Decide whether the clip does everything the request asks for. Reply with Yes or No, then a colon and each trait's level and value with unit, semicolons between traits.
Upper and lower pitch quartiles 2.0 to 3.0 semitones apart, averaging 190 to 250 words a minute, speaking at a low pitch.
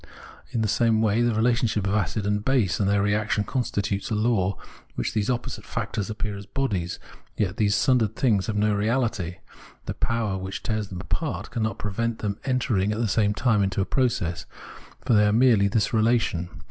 Yes: narrow, 2.6 semitones; average, 195 wpm; low, 105 Hz